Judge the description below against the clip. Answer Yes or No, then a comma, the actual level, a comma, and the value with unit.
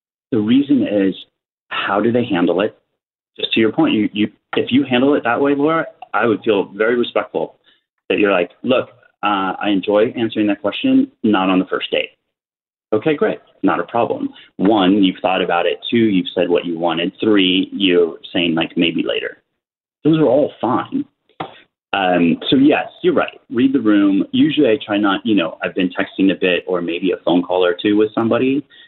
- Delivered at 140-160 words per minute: No, average, 195 wpm